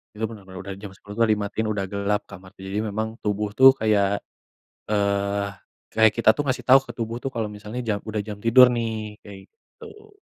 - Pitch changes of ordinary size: No, narrow, 2.2 semitones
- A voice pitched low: Yes, low, 105 Hz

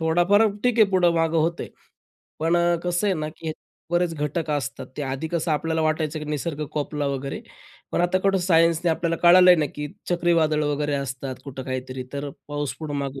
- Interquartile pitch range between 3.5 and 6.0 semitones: No, average, 3.0 semitones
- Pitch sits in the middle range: Yes, medium, 155 Hz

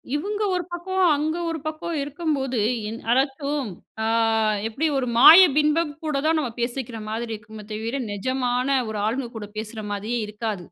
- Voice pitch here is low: No, very high, 260 Hz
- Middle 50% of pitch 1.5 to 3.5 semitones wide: No, wide, 5.6 semitones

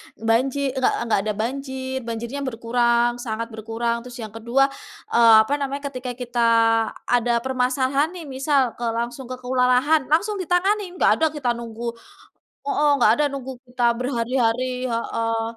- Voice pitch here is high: Yes, very high, 250 Hz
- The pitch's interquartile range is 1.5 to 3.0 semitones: Yes, narrow, 2.6 semitones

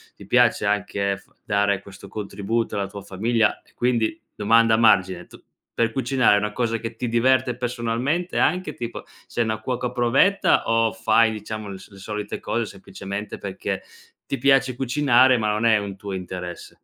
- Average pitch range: Yes, average, 3.2 semitones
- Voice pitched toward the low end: Yes, low, 110 Hz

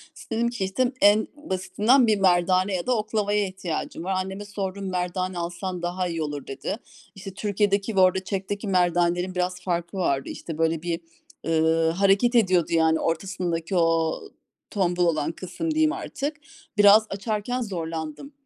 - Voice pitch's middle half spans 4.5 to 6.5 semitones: No, average, 3.0 semitones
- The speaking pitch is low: No, medium, 185 Hz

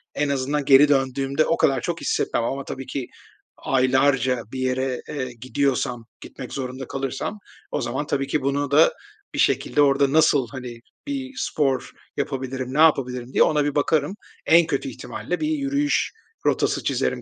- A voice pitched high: No, low, 135 Hz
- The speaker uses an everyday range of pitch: No, narrow, 2.2 semitones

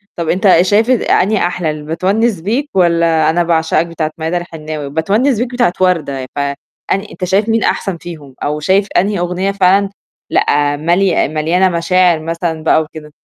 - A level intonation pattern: No, average, 3.6 semitones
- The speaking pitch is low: No, medium, 175 Hz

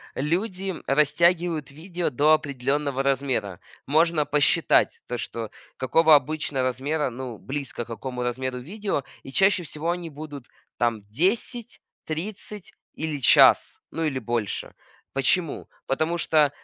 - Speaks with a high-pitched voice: No, medium, 145 Hz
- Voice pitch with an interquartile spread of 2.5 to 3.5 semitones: No, average, 4.3 semitones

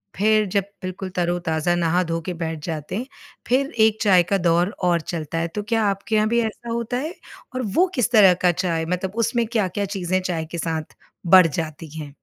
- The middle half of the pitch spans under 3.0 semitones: No, average, 4.4 semitones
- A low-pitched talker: No, medium, 185 Hz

